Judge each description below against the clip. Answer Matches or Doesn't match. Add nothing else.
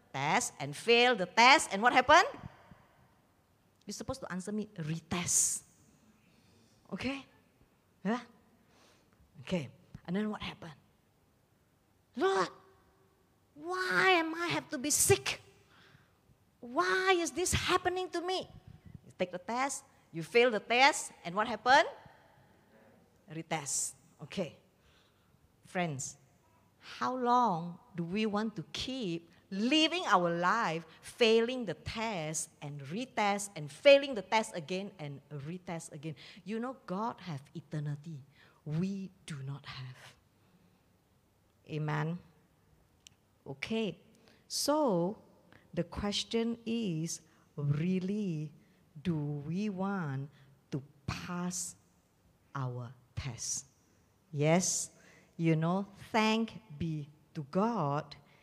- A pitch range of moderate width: Doesn't match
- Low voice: Doesn't match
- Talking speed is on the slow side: Matches